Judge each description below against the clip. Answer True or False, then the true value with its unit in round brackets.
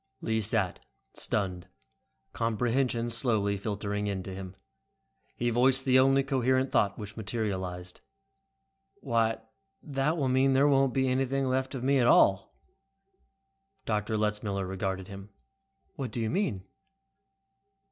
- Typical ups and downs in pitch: True (4.6 semitones)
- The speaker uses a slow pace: True (125 wpm)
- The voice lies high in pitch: False (115 Hz)